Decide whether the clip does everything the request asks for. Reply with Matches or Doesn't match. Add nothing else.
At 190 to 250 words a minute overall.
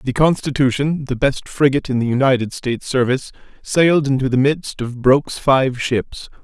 Doesn't match